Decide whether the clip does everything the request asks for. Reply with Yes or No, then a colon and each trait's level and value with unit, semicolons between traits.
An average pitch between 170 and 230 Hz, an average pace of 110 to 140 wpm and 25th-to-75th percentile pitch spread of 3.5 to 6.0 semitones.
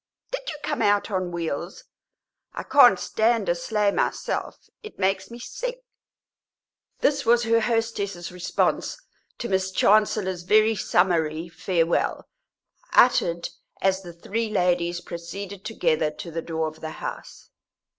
Yes: high, 190 Hz; slow, 135 wpm; average, 4.2 semitones